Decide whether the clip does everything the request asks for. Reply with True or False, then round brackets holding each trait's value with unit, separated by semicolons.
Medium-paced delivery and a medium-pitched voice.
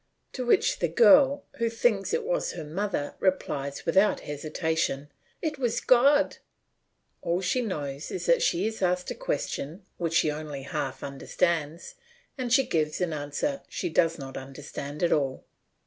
True (160 wpm; 170 Hz)